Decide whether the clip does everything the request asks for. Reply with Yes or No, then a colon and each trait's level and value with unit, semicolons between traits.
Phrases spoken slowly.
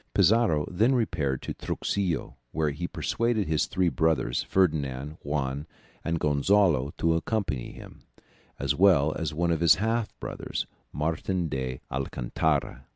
Yes: slow, 130 wpm